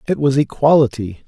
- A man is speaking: Yes, male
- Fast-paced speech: No, average, 140 wpm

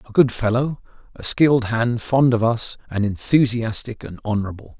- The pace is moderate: Yes, average, 165 wpm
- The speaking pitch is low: Yes, low, 115 Hz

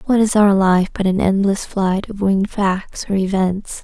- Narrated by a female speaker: Yes, female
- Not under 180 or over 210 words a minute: Yes, fast, 205 wpm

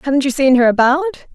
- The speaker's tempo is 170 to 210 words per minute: No, fast, 225 wpm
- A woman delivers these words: Yes, female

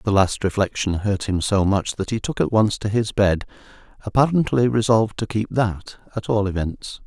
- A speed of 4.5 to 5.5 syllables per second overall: Yes, 4.9 syllables/s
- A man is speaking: Yes, male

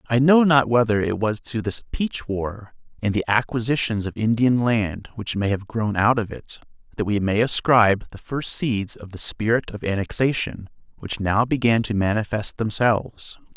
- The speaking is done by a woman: No, male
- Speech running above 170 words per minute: Yes, average, 180 wpm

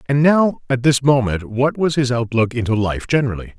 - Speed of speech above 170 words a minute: Yes, average, 200 wpm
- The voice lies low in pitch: Yes, low, 130 Hz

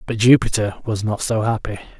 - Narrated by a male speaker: Yes, male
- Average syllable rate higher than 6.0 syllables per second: No, 5.5 syllables/s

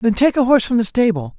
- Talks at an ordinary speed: No, fast, 305 wpm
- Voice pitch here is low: No, high, 225 Hz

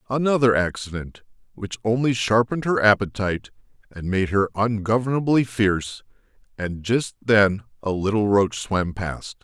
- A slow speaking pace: Yes, slow, 125 wpm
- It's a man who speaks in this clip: Yes, male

